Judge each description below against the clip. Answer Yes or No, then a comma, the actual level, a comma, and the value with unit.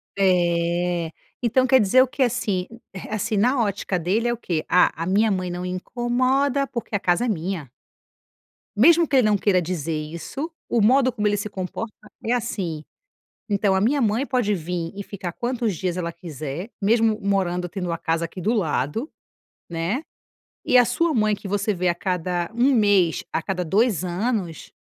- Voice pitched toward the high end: Yes, high, 200 Hz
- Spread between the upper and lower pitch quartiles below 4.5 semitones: No, average, 5.1 semitones